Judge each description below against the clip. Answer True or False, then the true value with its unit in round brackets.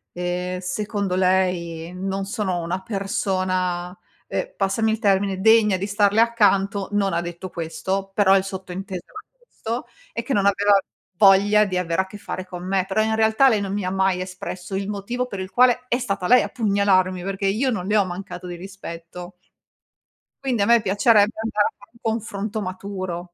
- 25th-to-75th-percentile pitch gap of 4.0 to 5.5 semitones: False (2.4 semitones)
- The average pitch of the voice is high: True (195 Hz)